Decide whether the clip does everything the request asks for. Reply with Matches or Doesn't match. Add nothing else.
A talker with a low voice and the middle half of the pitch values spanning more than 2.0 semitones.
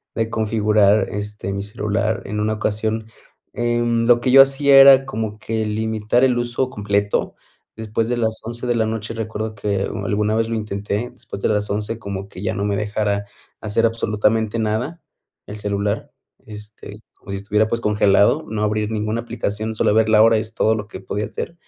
Doesn't match